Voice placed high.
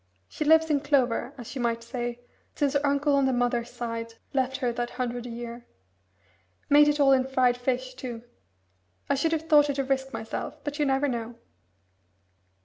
Yes: very high, 260 Hz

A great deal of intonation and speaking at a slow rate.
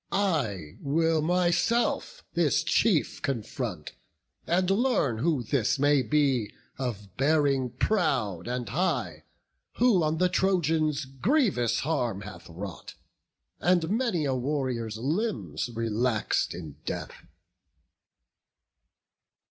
Yes: wide, 7.0 semitones; slow, 100 wpm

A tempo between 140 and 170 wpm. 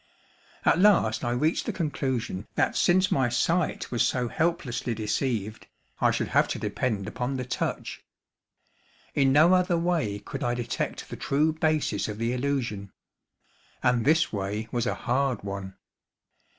Yes: average, 150 wpm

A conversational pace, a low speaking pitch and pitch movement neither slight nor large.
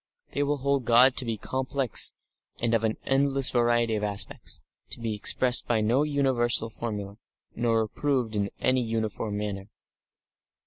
Yes: average, 150 wpm; low, 120 Hz; average, 3.3 semitones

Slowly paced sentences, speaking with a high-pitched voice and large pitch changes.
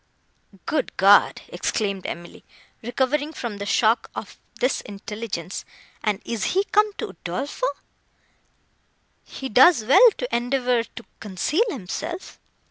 Yes: slow, 120 wpm; high, 235 Hz; wide, 6.4 semitones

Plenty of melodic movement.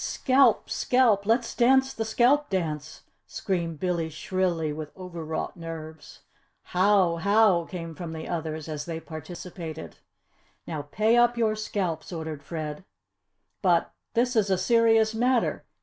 Yes: wide, 5.7 semitones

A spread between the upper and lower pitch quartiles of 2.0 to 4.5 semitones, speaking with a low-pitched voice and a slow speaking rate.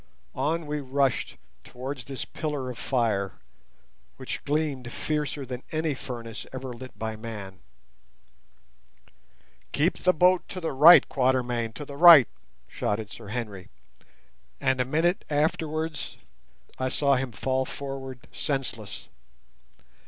Yes: average, 3.8 semitones; low, 130 Hz; slow, 120 wpm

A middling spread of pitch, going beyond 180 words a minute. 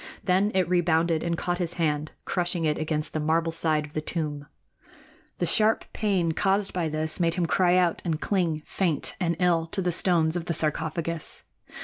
No: narrow, 2.2 semitones; average, 190 wpm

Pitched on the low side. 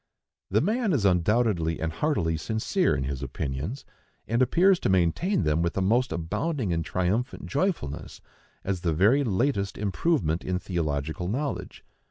Yes: very low, 95 Hz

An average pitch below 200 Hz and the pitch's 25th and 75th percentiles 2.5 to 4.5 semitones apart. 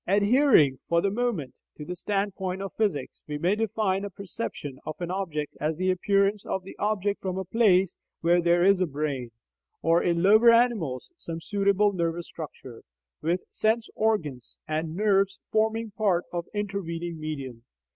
Yes: medium, 185 Hz; average, 3.9 semitones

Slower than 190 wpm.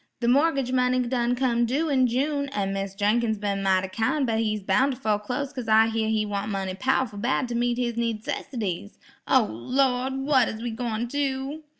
No: average, 195 wpm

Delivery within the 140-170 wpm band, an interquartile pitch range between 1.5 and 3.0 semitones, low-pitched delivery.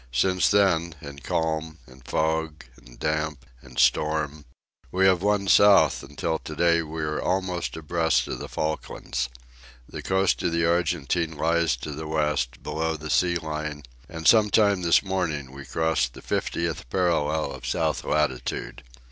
Yes: average, 155 wpm; narrow, 2.4 semitones; very low, 80 Hz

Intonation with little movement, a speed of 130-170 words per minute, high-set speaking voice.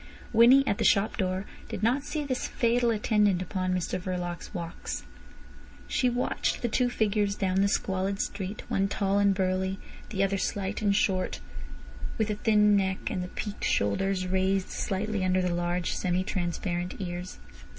Yes: narrow, 2.3 semitones; average, 165 wpm; high, 195 Hz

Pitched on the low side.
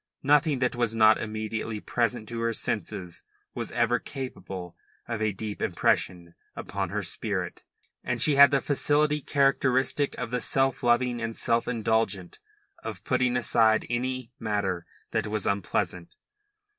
Yes: low, 115 Hz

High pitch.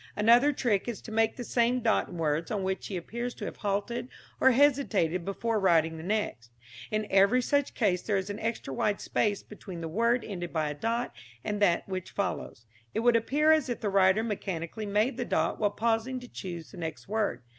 Yes: high, 210 Hz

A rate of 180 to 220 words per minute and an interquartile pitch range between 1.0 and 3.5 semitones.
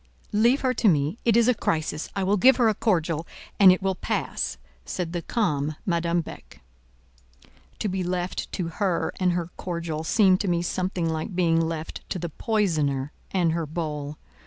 Yes: average, 185 wpm; average, 3.2 semitones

